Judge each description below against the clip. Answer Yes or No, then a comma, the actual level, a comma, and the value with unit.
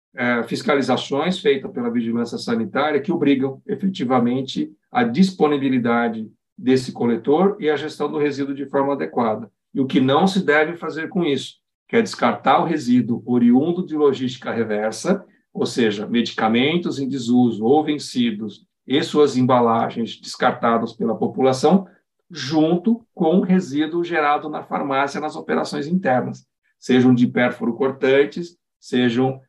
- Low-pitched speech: No, medium, 145 Hz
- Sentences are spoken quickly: No, average, 135 wpm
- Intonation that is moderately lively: No, wide, 6.2 semitones